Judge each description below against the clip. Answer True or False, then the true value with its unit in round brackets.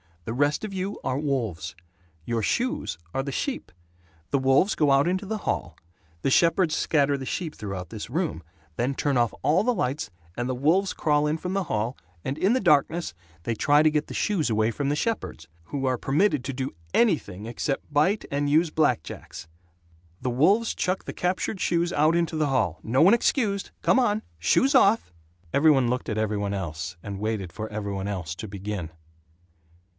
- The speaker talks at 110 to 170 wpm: False (195 wpm)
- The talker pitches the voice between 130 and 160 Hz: True (140 Hz)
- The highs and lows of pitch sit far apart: True (8.0 semitones)